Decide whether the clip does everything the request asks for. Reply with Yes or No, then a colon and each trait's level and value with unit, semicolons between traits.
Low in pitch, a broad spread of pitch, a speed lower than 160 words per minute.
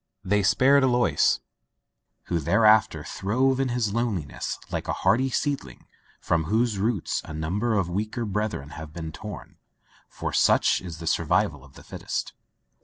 Yes: low, 105 Hz; wide, 6.1 semitones; average, 150 wpm